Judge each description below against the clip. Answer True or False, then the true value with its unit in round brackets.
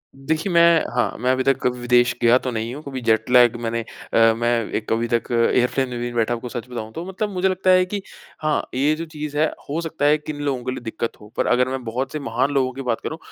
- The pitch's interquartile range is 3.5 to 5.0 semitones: True (4.2 semitones)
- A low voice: True (130 Hz)